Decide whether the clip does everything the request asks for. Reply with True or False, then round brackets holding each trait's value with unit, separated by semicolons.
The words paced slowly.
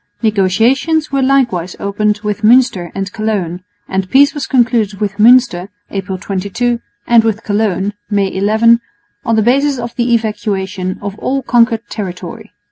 False (145 wpm)